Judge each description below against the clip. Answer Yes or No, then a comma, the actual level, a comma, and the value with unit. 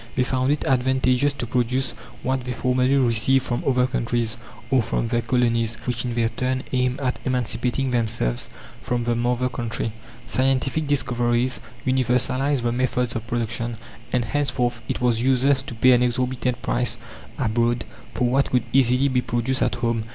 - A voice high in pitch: No, low, 125 Hz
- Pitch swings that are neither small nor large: No, narrow, 1.6 semitones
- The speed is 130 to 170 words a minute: Yes, average, 165 wpm